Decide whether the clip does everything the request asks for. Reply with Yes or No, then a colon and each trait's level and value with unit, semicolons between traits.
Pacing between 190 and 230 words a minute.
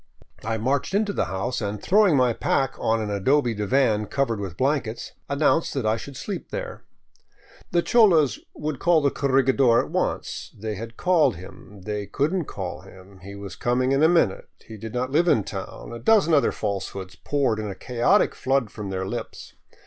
Yes: average, 195 wpm